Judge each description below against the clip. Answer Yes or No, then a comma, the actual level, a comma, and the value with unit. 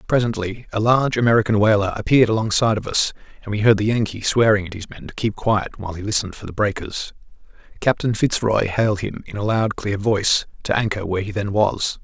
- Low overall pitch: Yes, low, 105 Hz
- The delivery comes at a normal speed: No, fast, 215 wpm